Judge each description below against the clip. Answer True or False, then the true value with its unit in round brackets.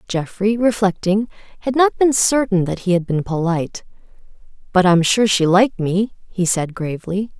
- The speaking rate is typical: True (170 wpm)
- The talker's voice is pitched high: True (195 Hz)